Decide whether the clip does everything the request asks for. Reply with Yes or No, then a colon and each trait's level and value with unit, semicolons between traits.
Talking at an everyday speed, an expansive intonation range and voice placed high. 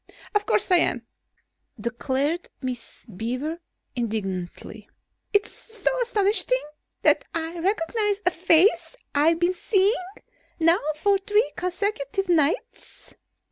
No: slow, 110 wpm; wide, 7.2 semitones; very high, 340 Hz